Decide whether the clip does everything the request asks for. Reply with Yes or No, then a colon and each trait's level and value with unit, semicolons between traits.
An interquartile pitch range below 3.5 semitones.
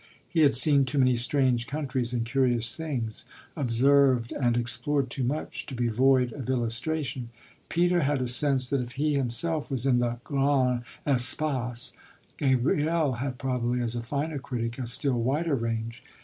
Yes: average, 2.9 semitones